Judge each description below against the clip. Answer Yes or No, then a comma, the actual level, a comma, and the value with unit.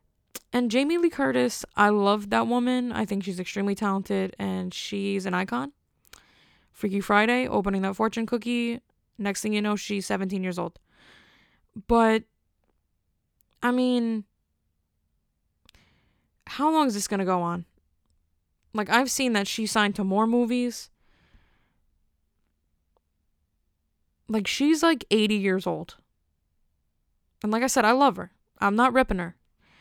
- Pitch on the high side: Yes, high, 200 Hz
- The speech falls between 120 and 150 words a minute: Yes, slow, 135 wpm